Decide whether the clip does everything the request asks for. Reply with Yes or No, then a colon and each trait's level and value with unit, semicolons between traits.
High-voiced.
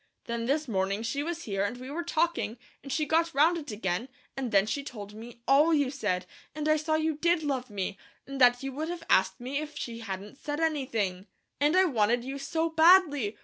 Yes: very high, 270 Hz